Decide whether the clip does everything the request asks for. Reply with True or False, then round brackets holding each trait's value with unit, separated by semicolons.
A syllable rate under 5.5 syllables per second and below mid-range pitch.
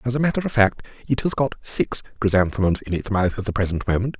False (6.4 syllables/s; 110 Hz)